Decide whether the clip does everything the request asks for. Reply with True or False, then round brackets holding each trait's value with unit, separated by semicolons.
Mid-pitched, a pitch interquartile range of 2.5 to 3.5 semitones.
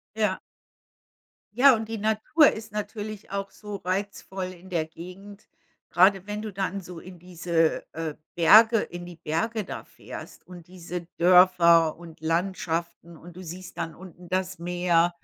True (180 Hz; 2.9 semitones)